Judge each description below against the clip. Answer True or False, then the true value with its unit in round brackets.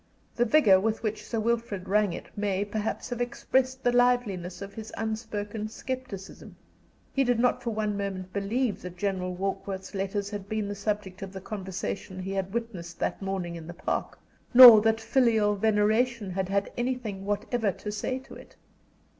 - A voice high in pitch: True (210 Hz)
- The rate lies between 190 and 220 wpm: False (175 wpm)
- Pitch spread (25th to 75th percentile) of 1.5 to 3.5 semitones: True (3.2 semitones)